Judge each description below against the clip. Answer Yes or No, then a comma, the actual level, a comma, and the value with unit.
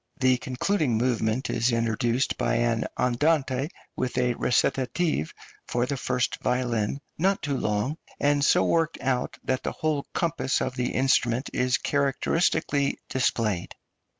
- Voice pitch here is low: Yes, low, 130 Hz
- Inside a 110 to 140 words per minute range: Yes, slow, 135 wpm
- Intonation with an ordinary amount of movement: Yes, average, 3.0 semitones